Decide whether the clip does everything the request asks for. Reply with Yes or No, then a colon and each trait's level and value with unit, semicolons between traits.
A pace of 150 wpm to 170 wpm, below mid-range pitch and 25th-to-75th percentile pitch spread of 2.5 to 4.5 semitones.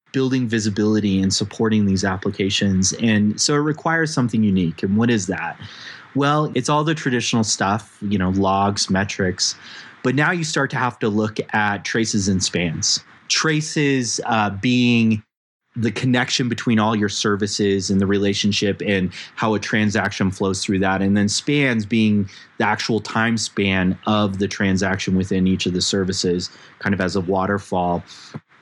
Yes: average, 165 wpm; low, 105 Hz; average, 3.1 semitones